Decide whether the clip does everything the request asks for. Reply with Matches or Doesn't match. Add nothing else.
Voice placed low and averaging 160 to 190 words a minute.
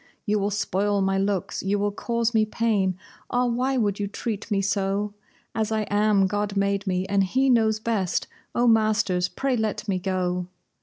Doesn't match